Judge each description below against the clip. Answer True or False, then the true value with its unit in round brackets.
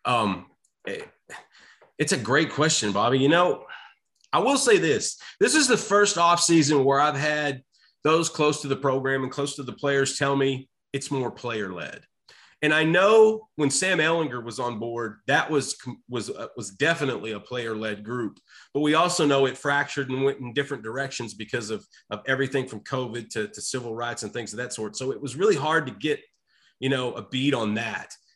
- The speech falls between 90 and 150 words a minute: False (205 wpm)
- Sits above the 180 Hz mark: False (140 Hz)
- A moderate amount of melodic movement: True (3.9 semitones)